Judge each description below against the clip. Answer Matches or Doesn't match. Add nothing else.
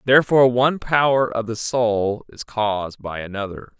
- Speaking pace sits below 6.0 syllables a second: Matches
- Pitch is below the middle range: Matches